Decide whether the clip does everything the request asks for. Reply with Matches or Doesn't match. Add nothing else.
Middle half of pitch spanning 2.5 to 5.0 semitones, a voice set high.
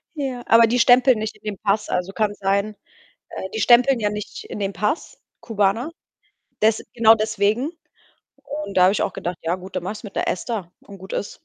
Matches